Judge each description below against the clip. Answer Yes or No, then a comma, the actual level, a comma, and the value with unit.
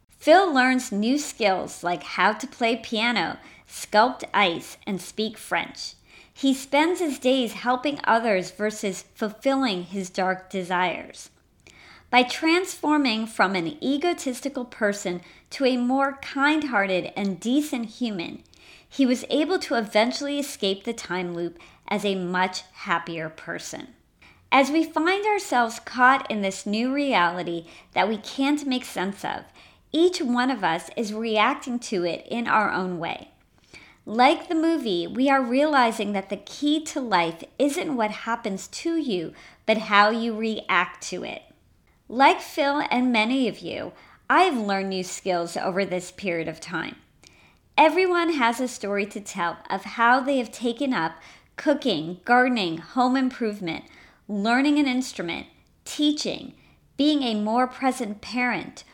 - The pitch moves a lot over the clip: Yes, wide, 5.8 semitones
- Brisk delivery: No, average, 145 wpm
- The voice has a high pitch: Yes, high, 235 Hz